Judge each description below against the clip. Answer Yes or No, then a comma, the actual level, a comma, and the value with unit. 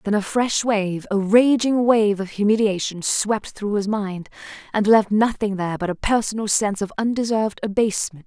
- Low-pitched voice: No, high, 210 Hz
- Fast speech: No, average, 175 wpm